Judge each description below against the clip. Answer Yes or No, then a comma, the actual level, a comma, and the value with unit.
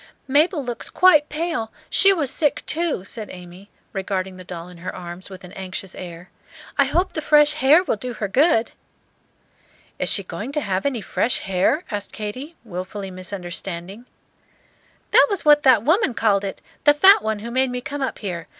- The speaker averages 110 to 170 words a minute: No, average, 185 wpm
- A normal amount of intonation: No, wide, 7.8 semitones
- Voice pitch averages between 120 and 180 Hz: No, high, 220 Hz